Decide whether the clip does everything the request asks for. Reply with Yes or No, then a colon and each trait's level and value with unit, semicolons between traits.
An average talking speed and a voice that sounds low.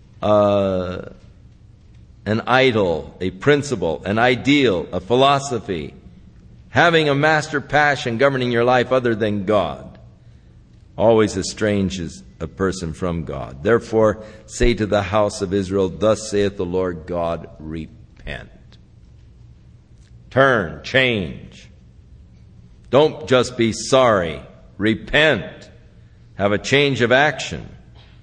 No: slow, 105 wpm; low, 110 Hz